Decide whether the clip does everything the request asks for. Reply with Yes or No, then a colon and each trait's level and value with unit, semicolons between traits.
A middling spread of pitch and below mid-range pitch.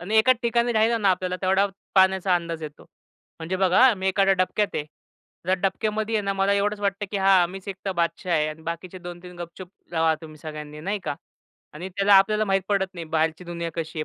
No: average, 3.0 semitones; high, 190 Hz